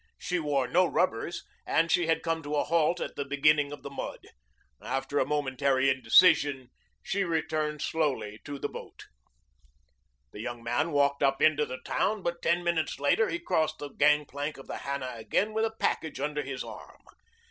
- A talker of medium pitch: Yes, medium, 145 Hz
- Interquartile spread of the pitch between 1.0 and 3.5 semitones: Yes, average, 3.2 semitones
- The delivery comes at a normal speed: Yes, average, 180 wpm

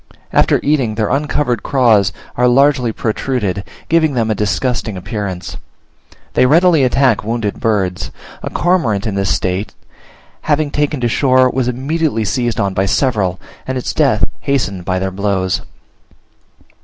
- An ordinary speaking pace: Yes, average, 145 wpm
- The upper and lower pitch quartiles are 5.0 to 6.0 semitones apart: Yes, wide, 5.4 semitones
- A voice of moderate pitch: No, low, 120 Hz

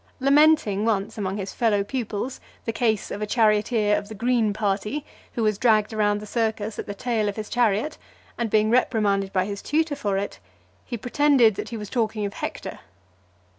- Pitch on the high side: Yes, high, 215 Hz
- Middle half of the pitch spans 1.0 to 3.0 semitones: Yes, narrow, 2.6 semitones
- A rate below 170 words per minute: No, average, 190 wpm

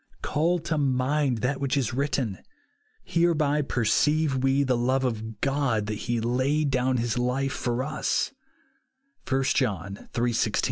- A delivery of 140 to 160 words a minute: Yes, average, 155 wpm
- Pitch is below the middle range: Yes, low, 130 Hz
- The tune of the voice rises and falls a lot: No, average, 3.3 semitones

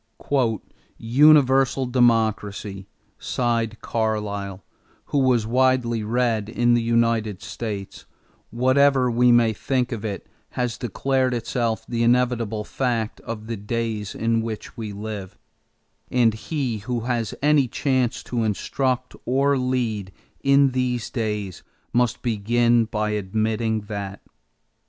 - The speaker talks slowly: Yes, slow, 120 wpm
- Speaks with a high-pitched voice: No, low, 115 Hz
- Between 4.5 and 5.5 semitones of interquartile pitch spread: No, narrow, 2.6 semitones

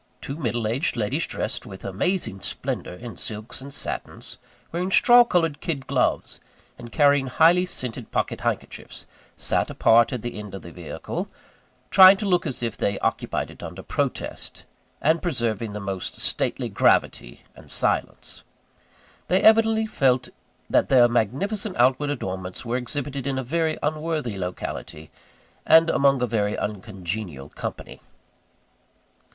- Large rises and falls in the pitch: Yes, wide, 7.3 semitones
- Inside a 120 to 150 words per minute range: Yes, average, 145 wpm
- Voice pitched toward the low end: Yes, low, 130 Hz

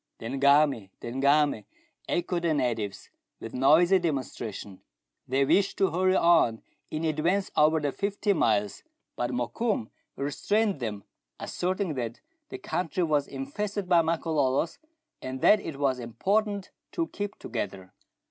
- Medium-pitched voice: Yes, medium, 150 Hz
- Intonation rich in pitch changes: Yes, wide, 6.7 semitones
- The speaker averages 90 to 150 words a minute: Yes, average, 140 wpm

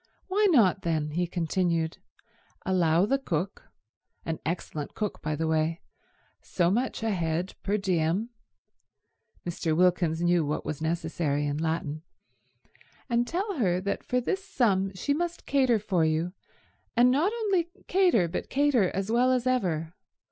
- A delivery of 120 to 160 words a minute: Yes, slow, 135 wpm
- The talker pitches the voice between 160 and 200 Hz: Yes, medium, 185 Hz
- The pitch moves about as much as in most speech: No, wide, 7.3 semitones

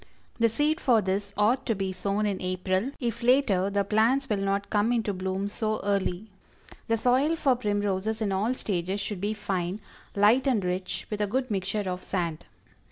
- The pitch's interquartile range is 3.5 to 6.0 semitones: No, average, 3.0 semitones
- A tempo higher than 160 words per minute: Yes, average, 185 wpm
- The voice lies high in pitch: Yes, high, 205 Hz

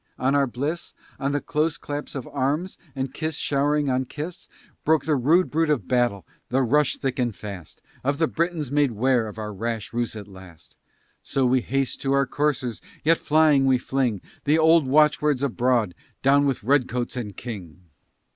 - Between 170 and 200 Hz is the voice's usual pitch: No, low, 135 Hz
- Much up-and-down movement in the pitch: No, average, 3.6 semitones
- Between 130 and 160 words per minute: No, average, 185 wpm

